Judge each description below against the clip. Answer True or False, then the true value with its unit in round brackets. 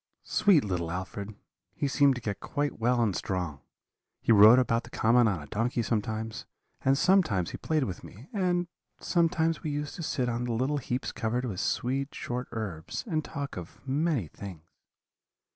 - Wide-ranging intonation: True (5.8 semitones)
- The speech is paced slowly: False (175 wpm)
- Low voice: True (120 Hz)